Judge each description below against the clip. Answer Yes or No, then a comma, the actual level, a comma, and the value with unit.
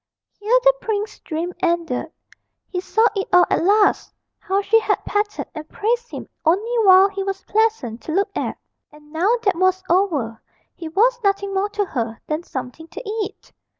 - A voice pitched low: No, very high, 390 Hz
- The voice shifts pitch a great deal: No, average, 4.2 semitones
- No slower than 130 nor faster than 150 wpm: No, average, 180 wpm